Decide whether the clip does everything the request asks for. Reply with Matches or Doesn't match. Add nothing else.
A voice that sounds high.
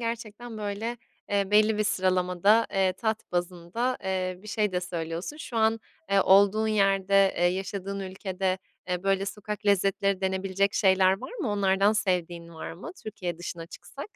Matches